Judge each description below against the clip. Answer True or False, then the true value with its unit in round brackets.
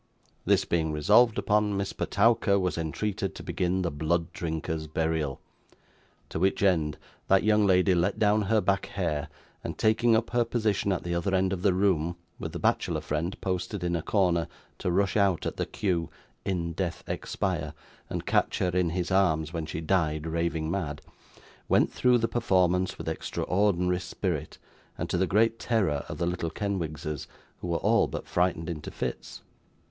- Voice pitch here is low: True (90 Hz)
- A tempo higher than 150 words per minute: True (175 wpm)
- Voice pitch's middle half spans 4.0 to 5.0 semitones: False (3.4 semitones)